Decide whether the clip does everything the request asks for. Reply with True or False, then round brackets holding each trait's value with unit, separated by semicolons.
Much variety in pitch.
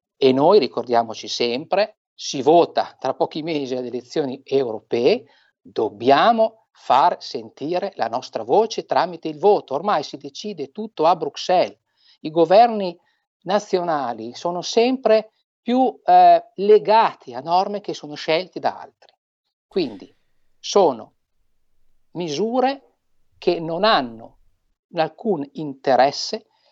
True (7.7 semitones)